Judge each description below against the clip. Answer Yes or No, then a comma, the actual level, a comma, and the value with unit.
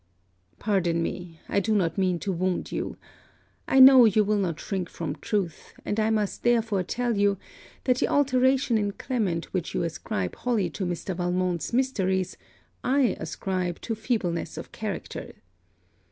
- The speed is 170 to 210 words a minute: No, average, 155 wpm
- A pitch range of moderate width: Yes, average, 4.5 semitones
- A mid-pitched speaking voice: No, high, 200 Hz